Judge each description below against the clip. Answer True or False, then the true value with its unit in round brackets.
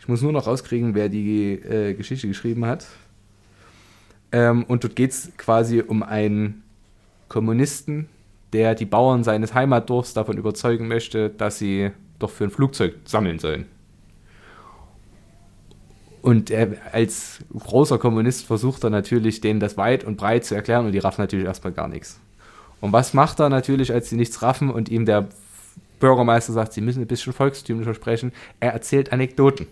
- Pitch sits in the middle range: False (115 Hz)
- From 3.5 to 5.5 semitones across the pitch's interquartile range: False (2.9 semitones)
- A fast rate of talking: False (165 wpm)